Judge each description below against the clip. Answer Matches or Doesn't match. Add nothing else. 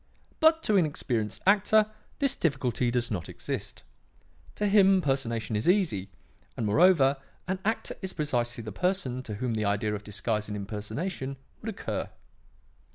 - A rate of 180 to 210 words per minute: Doesn't match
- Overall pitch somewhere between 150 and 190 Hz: Doesn't match